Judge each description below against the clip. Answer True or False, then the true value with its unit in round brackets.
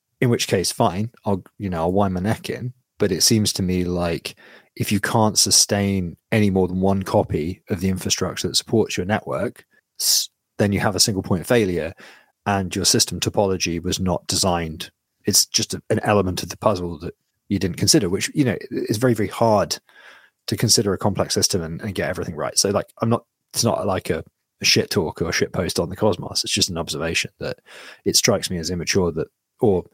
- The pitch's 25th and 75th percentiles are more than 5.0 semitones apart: False (2.9 semitones)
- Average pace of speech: False (210 wpm)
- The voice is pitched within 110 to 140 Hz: False (100 Hz)